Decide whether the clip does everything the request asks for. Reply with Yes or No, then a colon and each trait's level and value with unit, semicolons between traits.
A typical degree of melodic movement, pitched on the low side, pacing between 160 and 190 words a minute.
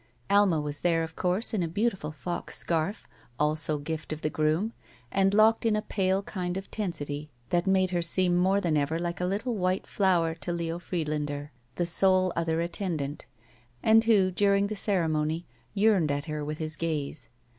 No: average, 3.7 semitones; medium, 175 Hz; average, 180 wpm